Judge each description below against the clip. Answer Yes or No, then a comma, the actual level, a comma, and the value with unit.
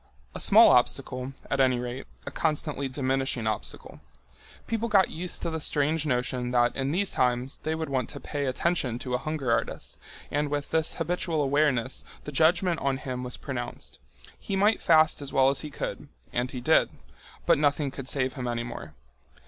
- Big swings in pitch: No, average, 3.8 semitones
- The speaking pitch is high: No, medium, 140 Hz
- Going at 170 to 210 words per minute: Yes, average, 180 wpm